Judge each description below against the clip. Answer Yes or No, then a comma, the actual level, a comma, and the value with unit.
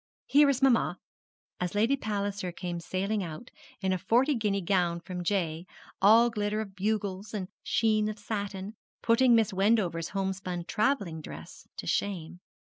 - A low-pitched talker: No, high, 200 Hz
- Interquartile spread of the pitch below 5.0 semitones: Yes, average, 3.3 semitones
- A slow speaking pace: No, average, 150 wpm